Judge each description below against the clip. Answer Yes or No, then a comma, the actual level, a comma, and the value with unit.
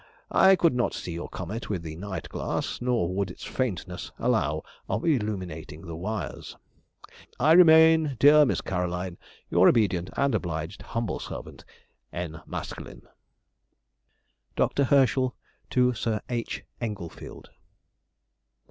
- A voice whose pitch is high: No, low, 105 Hz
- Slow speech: Yes, slow, 120 wpm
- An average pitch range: No, wide, 6.6 semitones